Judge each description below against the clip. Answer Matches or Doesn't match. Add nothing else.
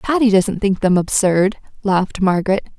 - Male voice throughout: Doesn't match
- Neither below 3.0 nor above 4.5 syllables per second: Doesn't match